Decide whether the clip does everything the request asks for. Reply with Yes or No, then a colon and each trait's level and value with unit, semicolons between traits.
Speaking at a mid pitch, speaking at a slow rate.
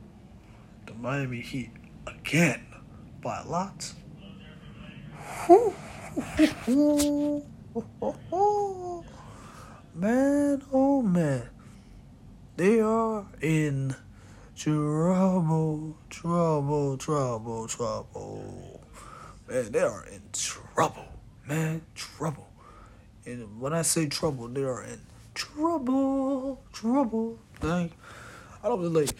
Yes: medium, 155 Hz; slow, 80 wpm